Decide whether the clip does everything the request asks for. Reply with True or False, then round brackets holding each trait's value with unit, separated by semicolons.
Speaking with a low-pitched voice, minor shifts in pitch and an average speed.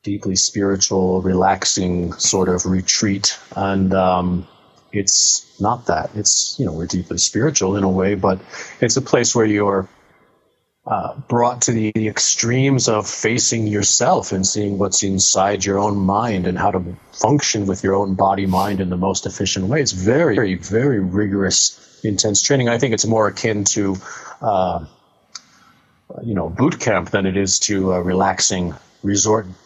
True (100 Hz; 2.3 semitones; 165 wpm)